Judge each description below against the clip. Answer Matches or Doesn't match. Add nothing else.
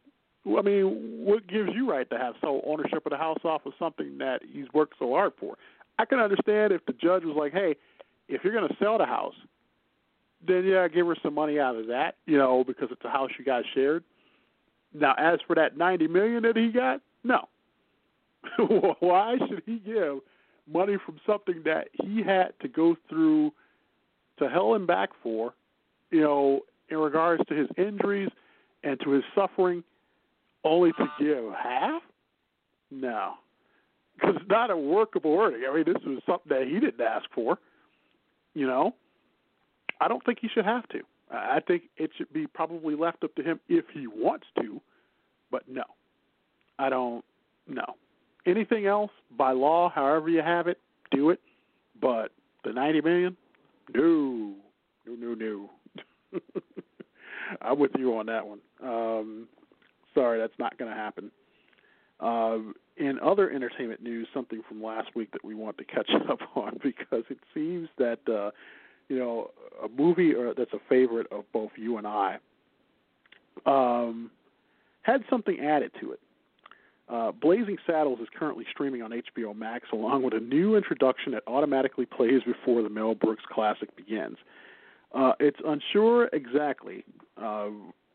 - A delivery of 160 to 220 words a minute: Matches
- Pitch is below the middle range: Doesn't match